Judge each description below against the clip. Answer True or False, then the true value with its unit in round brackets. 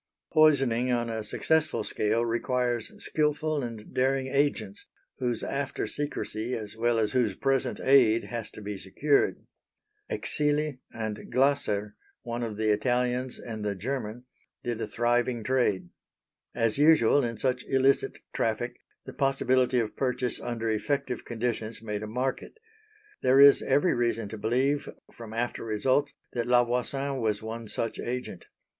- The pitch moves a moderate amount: True (3.1 semitones)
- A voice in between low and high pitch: False (120 Hz)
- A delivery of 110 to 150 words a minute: True (145 wpm)